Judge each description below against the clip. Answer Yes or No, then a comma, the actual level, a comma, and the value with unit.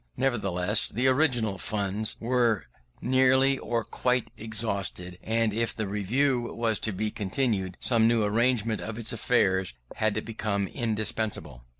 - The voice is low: Yes, low, 110 Hz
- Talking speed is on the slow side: Yes, slow, 130 wpm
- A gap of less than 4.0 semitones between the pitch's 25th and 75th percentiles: Yes, average, 3.0 semitones